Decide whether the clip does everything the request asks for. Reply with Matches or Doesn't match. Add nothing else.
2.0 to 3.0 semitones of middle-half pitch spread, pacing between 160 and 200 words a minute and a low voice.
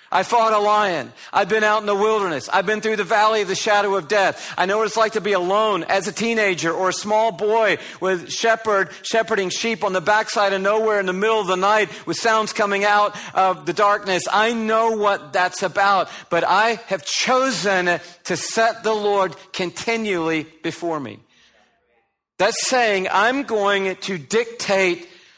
Doesn't match